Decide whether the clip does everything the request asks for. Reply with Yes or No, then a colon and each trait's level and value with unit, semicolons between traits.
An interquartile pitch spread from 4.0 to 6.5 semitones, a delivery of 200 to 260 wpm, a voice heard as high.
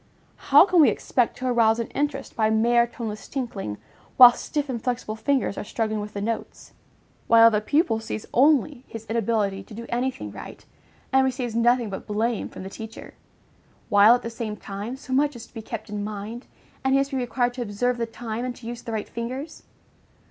No: average, 2.8 semitones; fast, 205 wpm; high, 235 Hz